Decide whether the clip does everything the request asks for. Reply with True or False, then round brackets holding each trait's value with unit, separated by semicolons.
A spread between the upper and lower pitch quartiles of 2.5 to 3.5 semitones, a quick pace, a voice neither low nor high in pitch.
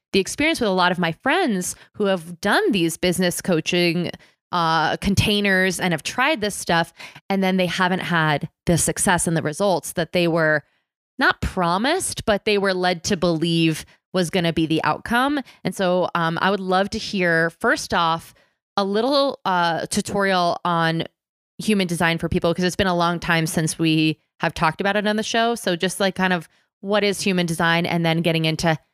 False (3.0 semitones; 195 wpm; 180 Hz)